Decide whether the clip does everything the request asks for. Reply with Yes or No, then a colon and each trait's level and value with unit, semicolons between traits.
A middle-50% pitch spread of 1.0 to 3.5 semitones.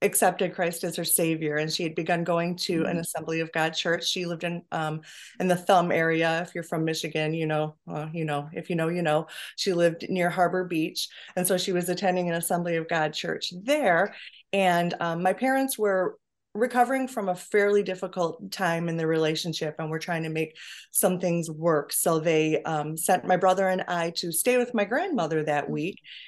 Yes: narrow, 2.4 semitones